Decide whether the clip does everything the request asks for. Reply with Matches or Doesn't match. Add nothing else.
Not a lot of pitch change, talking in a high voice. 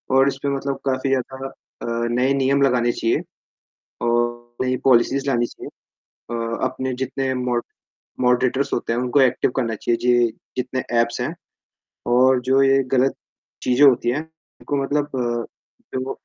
Doesn't match